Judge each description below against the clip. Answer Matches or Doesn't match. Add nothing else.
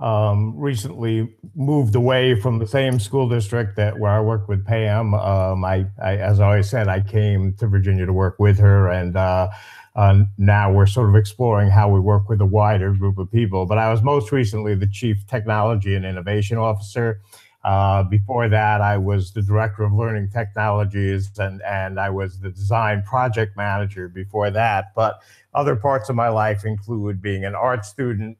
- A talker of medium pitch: Doesn't match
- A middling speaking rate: Matches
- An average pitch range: Doesn't match